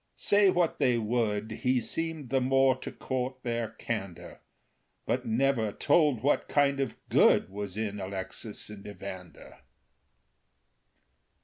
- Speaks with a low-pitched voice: Yes, low, 120 Hz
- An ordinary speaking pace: No, slow, 125 wpm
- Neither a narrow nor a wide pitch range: Yes, average, 4.8 semitones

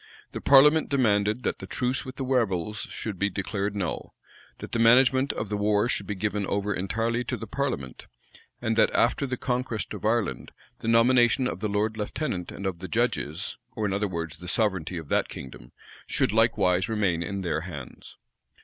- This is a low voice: Yes, low, 105 Hz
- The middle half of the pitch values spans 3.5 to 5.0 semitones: Yes, average, 4.1 semitones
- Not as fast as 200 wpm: Yes, average, 190 wpm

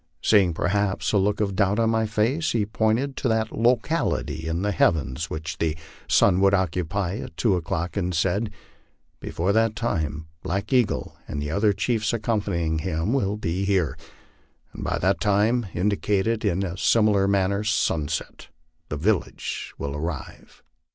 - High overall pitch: No, low, 100 Hz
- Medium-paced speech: Yes, average, 165 wpm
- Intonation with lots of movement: No, average, 4.1 semitones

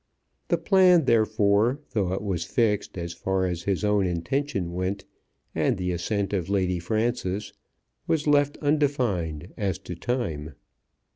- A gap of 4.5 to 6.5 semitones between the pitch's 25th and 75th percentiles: Yes, average, 5.2 semitones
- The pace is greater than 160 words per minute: No, average, 140 wpm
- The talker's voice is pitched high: No, low, 100 Hz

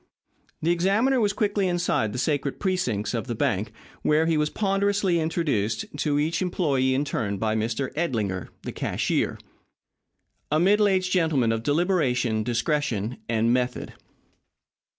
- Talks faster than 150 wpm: No, average, 140 wpm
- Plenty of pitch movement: Yes, wide, 7.5 semitones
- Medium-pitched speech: Yes, medium, 145 Hz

